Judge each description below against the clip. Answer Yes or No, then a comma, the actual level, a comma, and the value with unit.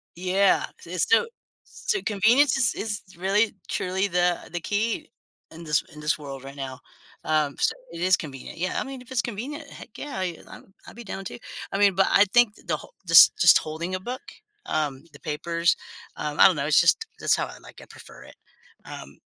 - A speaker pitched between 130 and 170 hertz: No, medium, 185 Hz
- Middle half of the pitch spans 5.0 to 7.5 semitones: Yes, wide, 5.6 semitones